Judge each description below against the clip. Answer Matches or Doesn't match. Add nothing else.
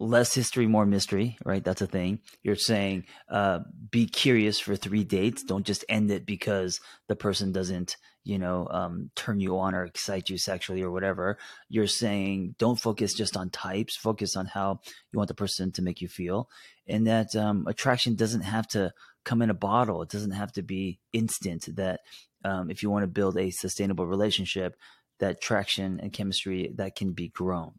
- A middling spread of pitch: Doesn't match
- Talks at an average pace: Matches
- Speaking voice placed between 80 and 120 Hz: Matches